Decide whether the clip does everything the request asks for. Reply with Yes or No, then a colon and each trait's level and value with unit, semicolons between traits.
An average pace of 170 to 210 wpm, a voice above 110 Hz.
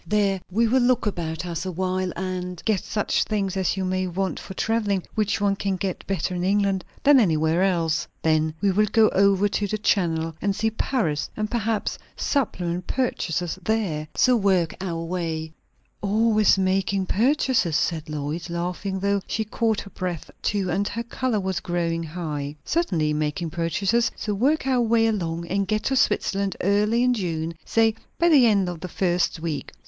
Yes: average, 180 wpm; high, 190 Hz